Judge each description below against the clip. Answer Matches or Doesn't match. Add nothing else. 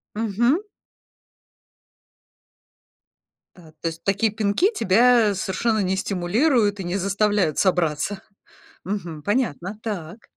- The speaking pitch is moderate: Doesn't match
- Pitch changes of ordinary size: Matches